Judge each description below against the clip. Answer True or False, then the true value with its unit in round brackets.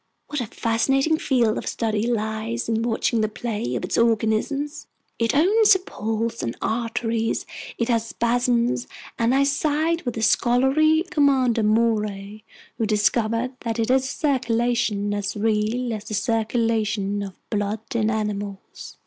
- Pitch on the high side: True (230 Hz)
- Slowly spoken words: False (150 wpm)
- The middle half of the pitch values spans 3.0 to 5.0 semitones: False (2.5 semitones)